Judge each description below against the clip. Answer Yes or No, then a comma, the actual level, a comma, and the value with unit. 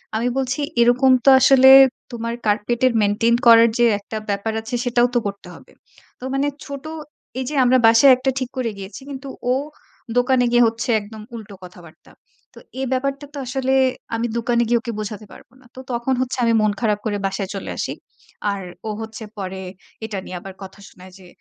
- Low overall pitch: No, high, 235 Hz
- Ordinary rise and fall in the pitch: Yes, average, 3.7 semitones